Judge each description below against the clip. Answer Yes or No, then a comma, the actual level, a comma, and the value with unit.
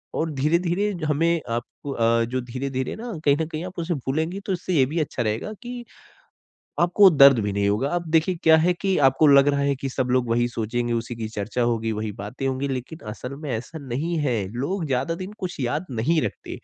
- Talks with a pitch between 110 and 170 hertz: Yes, medium, 140 Hz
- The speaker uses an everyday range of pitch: No, wide, 5.8 semitones